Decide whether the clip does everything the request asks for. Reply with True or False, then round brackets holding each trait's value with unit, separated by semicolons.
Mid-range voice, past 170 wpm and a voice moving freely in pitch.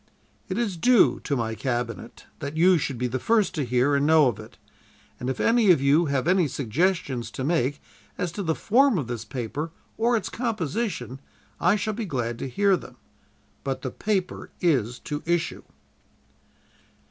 True (150 Hz; 180 wpm; 6.9 semitones)